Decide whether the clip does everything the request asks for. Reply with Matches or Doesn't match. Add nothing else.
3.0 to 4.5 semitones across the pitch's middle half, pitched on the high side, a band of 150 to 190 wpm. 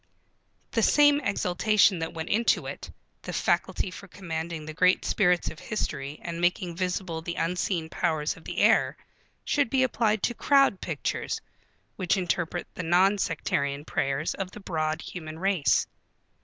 Doesn't match